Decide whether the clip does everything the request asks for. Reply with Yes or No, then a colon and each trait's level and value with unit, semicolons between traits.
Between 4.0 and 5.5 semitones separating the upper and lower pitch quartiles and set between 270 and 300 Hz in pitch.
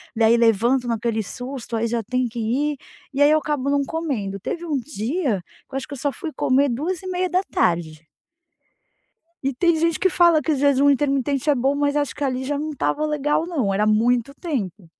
Yes: average, 4.3 semitones; very high, 275 Hz